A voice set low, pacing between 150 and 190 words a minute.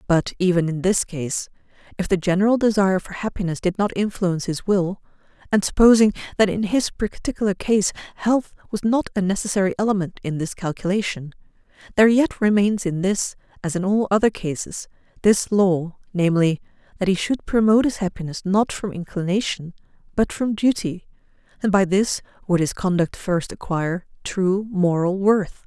No: high, 195 Hz; average, 160 wpm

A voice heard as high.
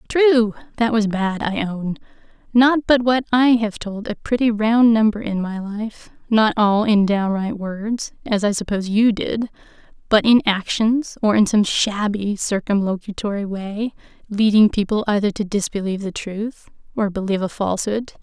Yes: high, 210 Hz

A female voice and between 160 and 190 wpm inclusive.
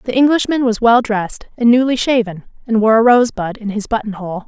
No: female; average, 200 wpm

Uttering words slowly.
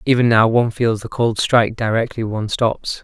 No: average, 200 wpm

